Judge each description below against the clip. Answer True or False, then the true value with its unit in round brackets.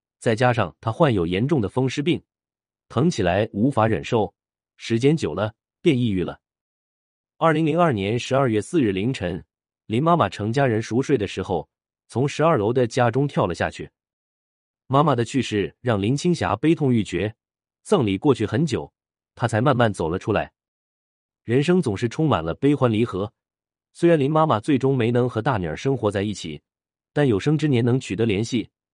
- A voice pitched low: True (120 Hz)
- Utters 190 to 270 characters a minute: True (265 characters per minute)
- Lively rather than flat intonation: True (5.7 semitones)